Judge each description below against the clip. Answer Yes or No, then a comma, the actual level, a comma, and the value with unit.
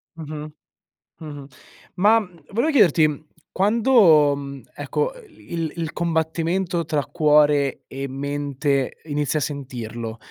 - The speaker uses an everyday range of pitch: Yes, average, 3.2 semitones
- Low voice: No, medium, 150 Hz